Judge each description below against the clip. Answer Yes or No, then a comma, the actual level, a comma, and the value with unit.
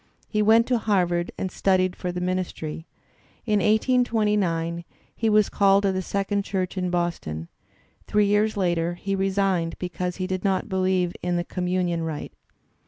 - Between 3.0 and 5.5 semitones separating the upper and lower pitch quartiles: No, narrow, 2.6 semitones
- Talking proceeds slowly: No, average, 160 wpm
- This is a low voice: No, medium, 185 Hz